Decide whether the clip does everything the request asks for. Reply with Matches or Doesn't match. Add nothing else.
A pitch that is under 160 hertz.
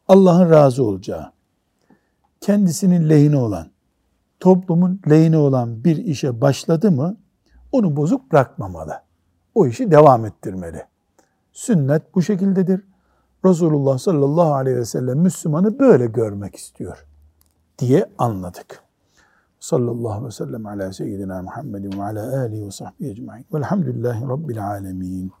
Matches